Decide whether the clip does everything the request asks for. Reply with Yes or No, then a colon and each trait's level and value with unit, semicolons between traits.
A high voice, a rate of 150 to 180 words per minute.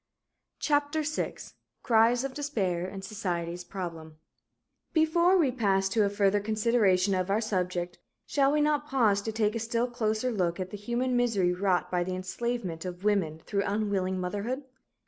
Yes: high, 205 Hz; average, 165 wpm